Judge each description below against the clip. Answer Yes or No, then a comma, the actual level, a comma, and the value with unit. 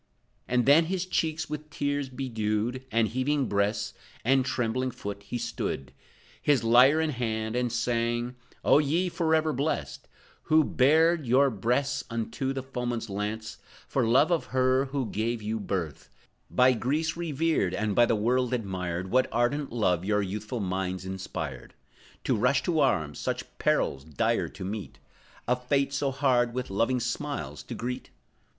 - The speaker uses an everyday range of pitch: Yes, average, 4.4 semitones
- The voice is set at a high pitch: No, low, 125 Hz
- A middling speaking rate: Yes, average, 155 wpm